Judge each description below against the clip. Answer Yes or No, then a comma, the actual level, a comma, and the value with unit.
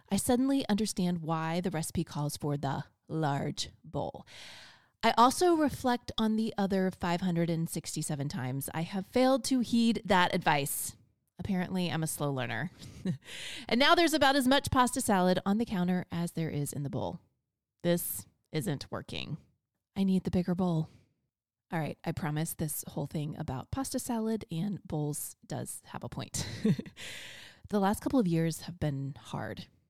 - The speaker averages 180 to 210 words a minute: No, average, 160 wpm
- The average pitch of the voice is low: No, medium, 180 Hz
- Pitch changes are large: Yes, wide, 6.0 semitones